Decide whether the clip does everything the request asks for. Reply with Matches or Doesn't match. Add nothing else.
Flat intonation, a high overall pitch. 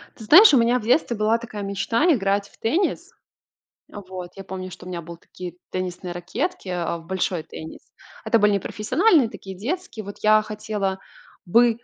Doesn't match